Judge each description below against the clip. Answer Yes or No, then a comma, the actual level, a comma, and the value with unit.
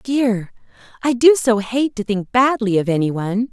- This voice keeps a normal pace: Yes, average, 155 wpm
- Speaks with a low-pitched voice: No, high, 225 Hz